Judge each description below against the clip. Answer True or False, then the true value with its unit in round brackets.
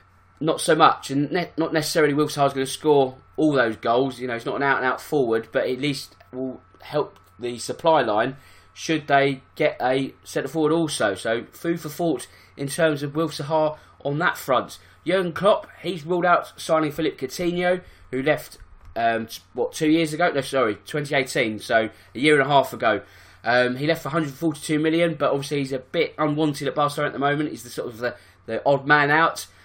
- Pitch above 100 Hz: True (140 Hz)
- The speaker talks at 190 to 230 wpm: True (200 wpm)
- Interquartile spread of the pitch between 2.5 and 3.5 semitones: False (4.3 semitones)